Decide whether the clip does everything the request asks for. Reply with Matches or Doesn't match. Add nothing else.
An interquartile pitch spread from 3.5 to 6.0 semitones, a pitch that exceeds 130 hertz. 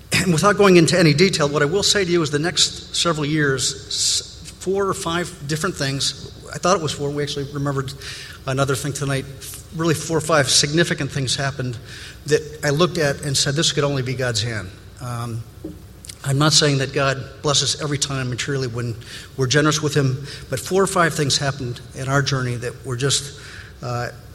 Doesn't match